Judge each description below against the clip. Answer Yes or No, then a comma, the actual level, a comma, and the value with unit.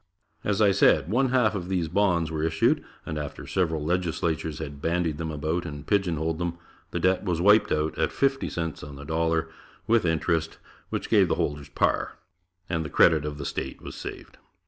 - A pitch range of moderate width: Yes, average, 3.0 semitones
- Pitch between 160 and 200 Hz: No, very low, 80 Hz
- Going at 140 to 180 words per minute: No, average, 190 wpm